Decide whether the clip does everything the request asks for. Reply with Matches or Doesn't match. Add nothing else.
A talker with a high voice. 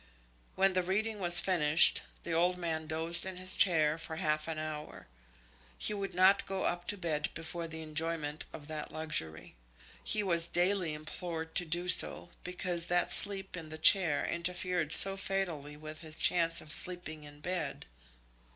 Doesn't match